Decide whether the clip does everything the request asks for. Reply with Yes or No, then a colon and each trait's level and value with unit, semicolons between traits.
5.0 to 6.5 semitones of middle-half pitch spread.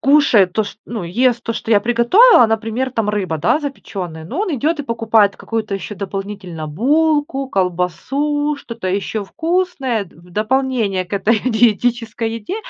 Yes: average, 5.3 semitones